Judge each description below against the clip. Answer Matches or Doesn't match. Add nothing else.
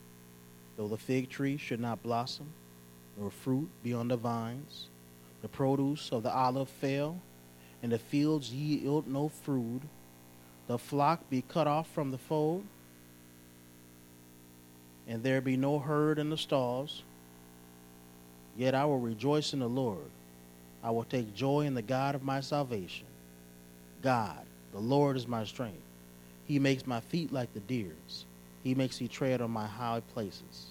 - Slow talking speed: Doesn't match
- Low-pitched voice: Matches